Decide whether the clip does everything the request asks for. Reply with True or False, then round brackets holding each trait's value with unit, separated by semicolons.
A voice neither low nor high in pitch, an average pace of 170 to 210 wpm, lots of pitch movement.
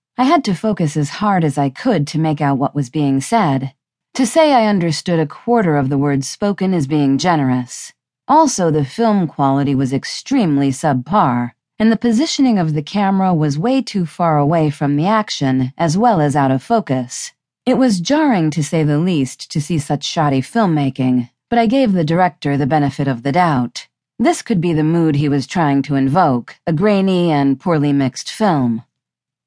True (155 Hz; 190 wpm; 6.5 semitones)